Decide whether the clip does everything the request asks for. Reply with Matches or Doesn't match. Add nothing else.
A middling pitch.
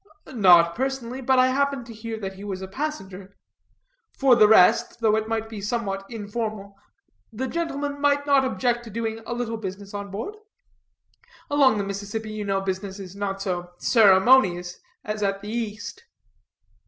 Doesn't match